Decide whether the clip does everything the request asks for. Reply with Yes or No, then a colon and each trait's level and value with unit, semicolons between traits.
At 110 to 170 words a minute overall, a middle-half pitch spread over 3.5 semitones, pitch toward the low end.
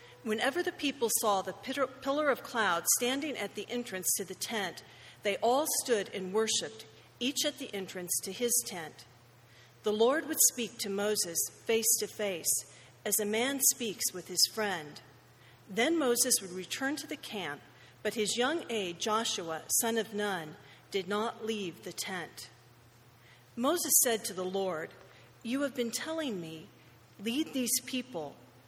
No: average, 160 wpm; average, 5.3 semitones; high, 215 Hz